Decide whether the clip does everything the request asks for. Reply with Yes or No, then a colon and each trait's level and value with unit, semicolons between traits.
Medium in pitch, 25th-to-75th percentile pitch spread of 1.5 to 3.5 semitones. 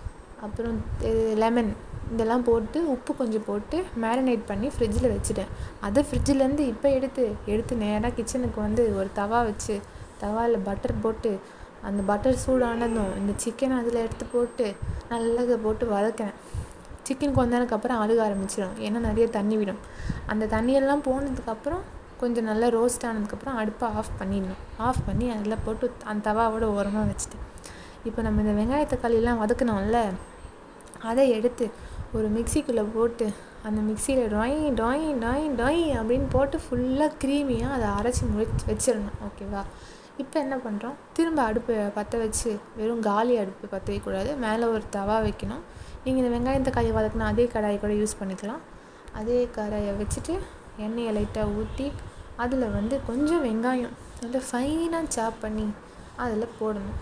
No: high, 230 Hz; average, 2.9 semitones